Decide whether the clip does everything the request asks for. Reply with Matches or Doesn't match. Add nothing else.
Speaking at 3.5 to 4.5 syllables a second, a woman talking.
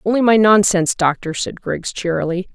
Doesn't match